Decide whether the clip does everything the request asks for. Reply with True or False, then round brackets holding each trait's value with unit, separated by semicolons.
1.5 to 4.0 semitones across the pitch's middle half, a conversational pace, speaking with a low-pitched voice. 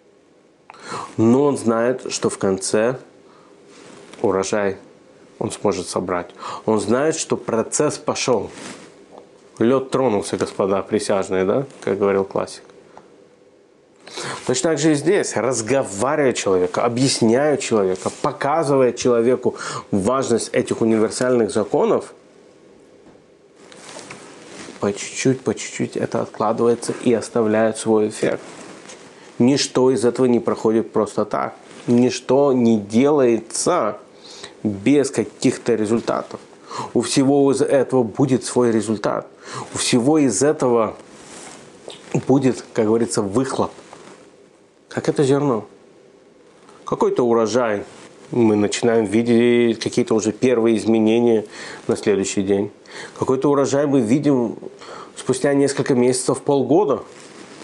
False (3.3 semitones; 105 wpm; 120 Hz)